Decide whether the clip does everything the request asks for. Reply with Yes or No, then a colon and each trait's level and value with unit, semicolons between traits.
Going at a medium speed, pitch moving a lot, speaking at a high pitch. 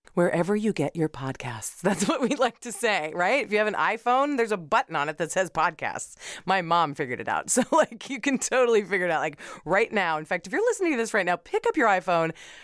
No: fast, 255 wpm; wide, 6.4 semitones; high, 200 Hz